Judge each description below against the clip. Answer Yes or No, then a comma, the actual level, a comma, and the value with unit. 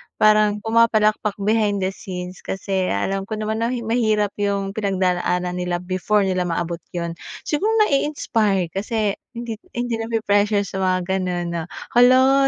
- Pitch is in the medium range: No, high, 205 Hz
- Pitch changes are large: No, average, 3.2 semitones